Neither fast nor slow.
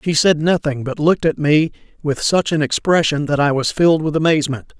No: fast, 215 wpm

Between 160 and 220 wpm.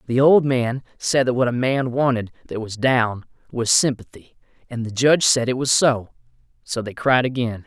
Yes: average, 195 wpm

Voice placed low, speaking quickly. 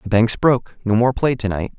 Yes: low, 115 Hz; fast, 270 wpm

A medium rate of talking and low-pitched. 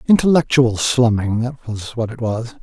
Yes: average, 160 wpm; low, 120 Hz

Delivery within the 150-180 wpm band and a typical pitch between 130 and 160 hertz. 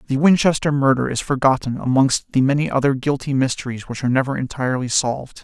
Yes: average, 175 wpm; low, 135 Hz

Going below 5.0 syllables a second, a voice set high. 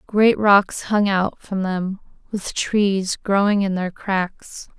Yes: 3.1 syllables/s; high, 195 Hz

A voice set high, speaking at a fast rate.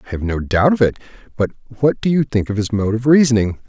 No: low, 115 Hz; fast, 260 wpm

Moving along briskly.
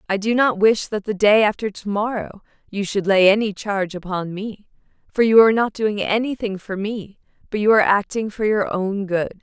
Yes: fast, 210 wpm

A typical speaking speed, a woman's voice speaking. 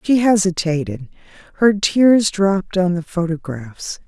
No: slow, 120 wpm; female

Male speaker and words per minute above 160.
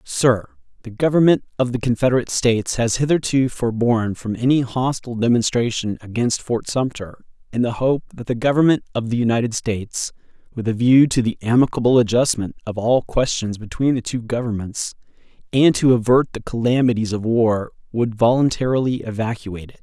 No: male; average, 155 wpm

